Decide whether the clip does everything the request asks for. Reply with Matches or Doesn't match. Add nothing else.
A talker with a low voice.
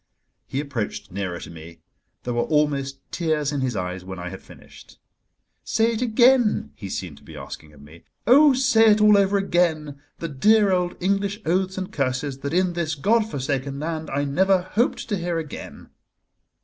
Doesn't match